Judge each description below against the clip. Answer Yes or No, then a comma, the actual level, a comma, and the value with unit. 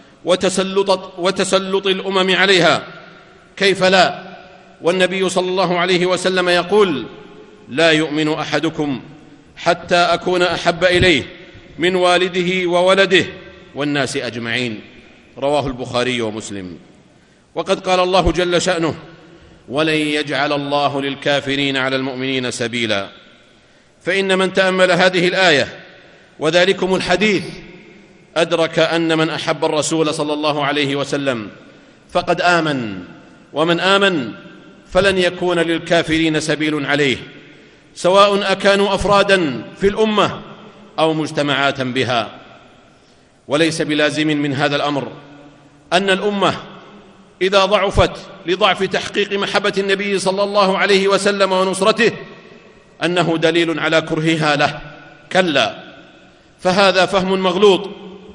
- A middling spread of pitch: Yes, average, 4.1 semitones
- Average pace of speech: Yes, average, 100 wpm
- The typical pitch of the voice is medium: Yes, medium, 175 Hz